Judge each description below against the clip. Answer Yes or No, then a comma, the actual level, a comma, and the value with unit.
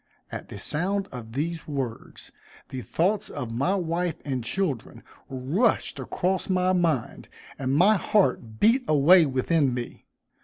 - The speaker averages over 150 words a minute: No, average, 140 wpm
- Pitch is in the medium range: Yes, medium, 155 Hz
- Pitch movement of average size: No, wide, 6.1 semitones